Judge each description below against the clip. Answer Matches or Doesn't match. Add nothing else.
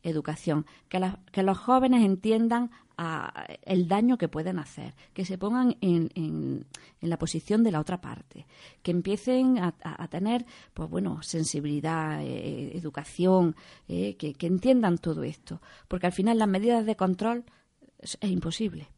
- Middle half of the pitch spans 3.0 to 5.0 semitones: Doesn't match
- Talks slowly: Doesn't match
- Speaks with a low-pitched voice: Doesn't match